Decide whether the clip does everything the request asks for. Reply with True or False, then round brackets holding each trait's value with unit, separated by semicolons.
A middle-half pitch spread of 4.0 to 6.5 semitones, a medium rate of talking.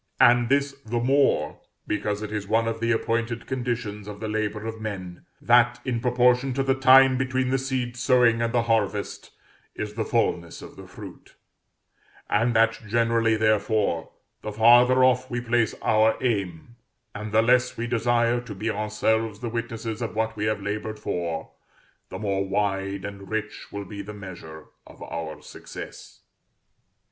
False (2.7 semitones; 165 wpm)